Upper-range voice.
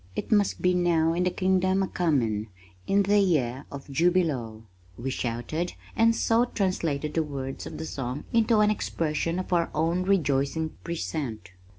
No: medium, 165 Hz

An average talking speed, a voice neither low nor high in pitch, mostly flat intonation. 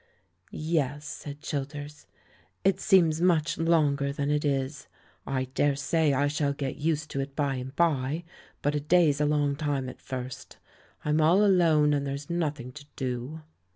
Yes: average, 160 wpm; medium, 145 Hz; narrow, 2.0 semitones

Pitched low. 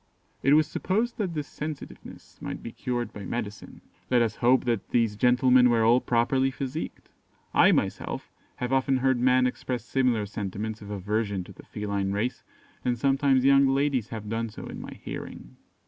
Yes: low, 125 Hz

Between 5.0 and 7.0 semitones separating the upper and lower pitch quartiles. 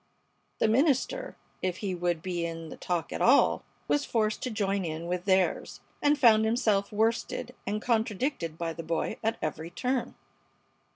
Yes: average, 5.3 semitones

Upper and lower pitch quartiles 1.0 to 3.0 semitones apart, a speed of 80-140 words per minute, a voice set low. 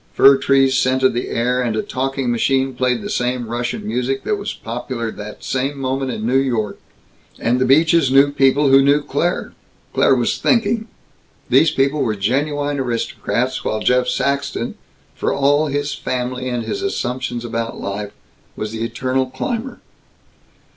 No: narrow, 2.4 semitones; average, 160 wpm; low, 130 Hz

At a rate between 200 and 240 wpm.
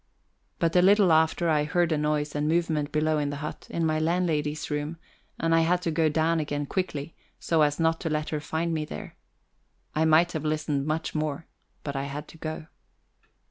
Yes: fast, 205 wpm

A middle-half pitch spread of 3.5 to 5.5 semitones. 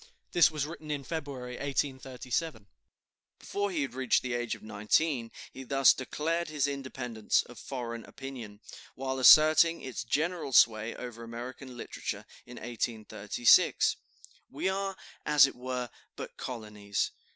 Yes: average, 4.0 semitones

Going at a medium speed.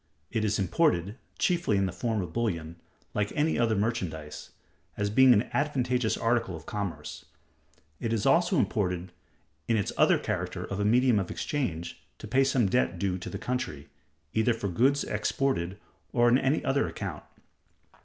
Yes: average, 165 wpm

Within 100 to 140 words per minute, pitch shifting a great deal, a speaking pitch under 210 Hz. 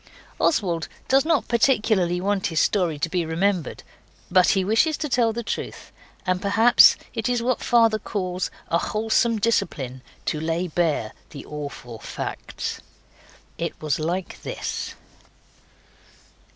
Yes: slow, 135 wpm; wide, 5.7 semitones; high, 190 Hz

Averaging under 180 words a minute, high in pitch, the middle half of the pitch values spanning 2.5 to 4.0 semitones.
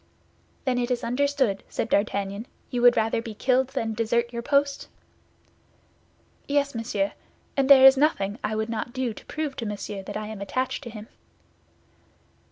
Yes: average, 170 wpm; high, 235 Hz; average, 3.6 semitones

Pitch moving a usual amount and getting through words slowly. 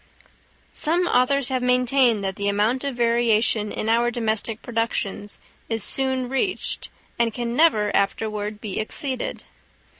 Yes: average, 3.2 semitones; slow, 130 wpm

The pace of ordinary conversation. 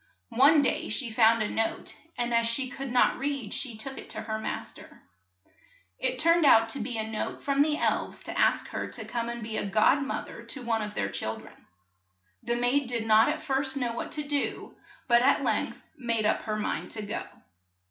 No: fast, 215 wpm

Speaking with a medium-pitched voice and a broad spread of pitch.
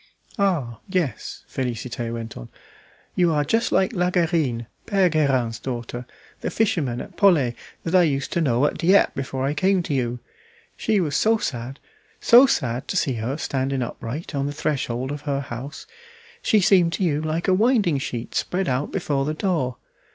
Yes: medium, 145 Hz; wide, 6.0 semitones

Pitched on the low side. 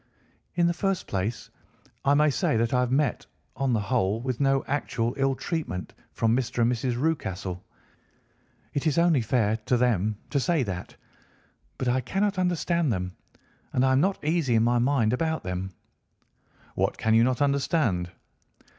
Yes: low, 125 Hz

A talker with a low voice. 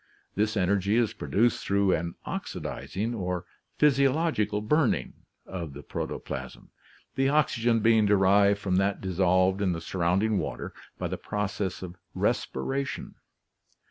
Yes: low, 100 Hz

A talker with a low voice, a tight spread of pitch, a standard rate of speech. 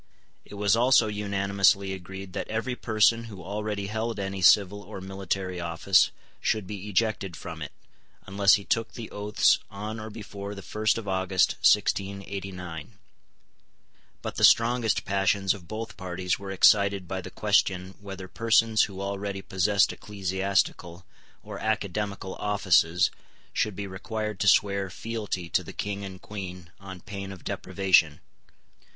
Yes: low, 100 Hz; narrow, 1.9 semitones; average, 145 wpm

